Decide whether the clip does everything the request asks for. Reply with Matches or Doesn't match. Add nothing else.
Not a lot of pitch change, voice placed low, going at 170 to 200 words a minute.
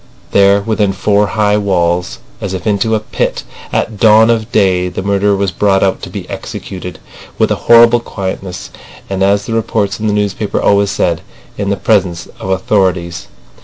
Matches